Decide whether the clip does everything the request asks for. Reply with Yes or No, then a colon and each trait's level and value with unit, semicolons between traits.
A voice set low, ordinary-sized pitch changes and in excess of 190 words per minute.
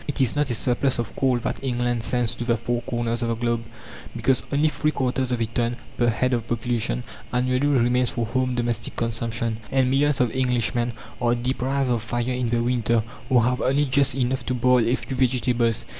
No: low, 120 Hz; narrow, 1.6 semitones; fast, 205 wpm